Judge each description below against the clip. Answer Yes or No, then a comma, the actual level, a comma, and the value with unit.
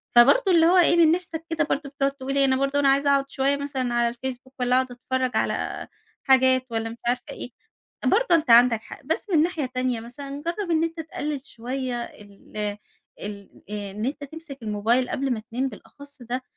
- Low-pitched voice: No, very high, 265 Hz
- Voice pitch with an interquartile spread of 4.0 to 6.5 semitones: No, average, 3.2 semitones